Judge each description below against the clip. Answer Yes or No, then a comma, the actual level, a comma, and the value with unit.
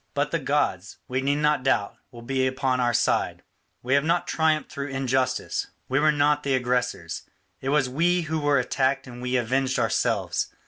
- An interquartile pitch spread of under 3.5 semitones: Yes, narrow, 2.6 semitones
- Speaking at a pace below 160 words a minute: No, average, 185 wpm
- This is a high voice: No, low, 135 Hz